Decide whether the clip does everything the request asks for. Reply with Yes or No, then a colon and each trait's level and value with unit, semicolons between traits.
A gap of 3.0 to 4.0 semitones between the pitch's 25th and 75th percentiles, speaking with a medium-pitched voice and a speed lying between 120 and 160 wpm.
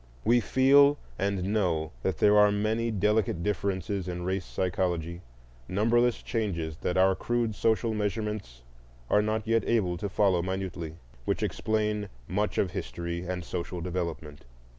No: average, 3.5 semitones; low, 100 Hz; average, 140 wpm